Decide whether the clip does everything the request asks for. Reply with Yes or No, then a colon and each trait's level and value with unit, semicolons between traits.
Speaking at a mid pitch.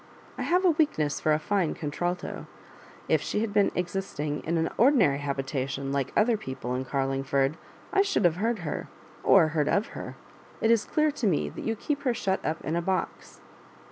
Yes: medium, 170 Hz